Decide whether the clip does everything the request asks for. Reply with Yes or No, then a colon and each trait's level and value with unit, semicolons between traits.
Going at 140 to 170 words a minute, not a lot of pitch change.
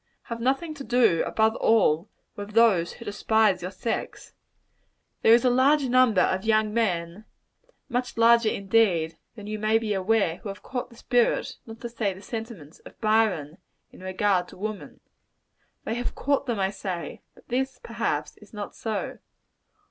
No: average, 165 wpm; average, 3.4 semitones